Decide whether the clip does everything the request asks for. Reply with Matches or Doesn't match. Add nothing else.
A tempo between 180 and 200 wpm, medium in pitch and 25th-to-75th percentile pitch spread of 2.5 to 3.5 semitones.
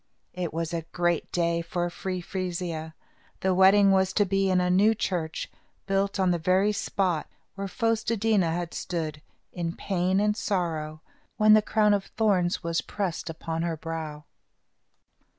Doesn't match